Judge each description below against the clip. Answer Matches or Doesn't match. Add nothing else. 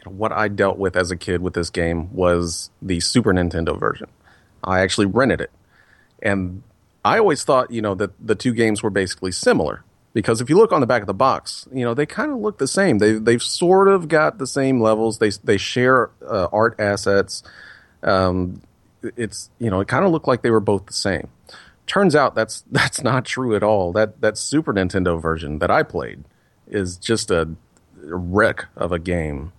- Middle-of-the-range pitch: Doesn't match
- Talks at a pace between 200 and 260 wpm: Matches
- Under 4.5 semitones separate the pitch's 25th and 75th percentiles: Doesn't match